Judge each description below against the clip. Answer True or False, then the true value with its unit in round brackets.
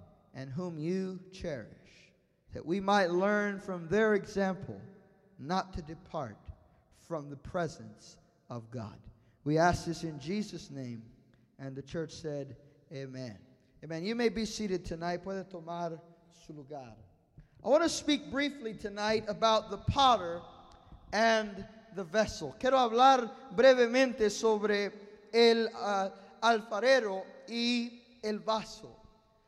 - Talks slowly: True (125 wpm)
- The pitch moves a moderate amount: False (6.3 semitones)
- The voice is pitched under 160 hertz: False (190 Hz)